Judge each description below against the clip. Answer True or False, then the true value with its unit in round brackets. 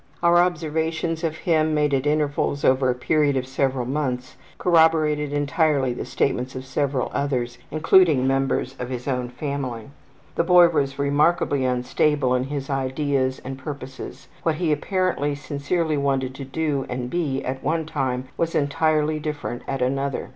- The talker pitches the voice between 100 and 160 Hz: True (140 Hz)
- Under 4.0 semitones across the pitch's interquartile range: True (3.0 semitones)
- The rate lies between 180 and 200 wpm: False (155 wpm)